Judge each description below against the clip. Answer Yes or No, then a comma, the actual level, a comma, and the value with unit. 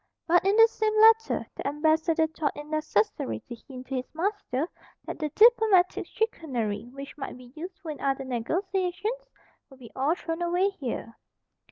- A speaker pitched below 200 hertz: No, very high, 320 Hz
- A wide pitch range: Yes, wide, 6.3 semitones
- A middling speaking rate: Yes, average, 165 wpm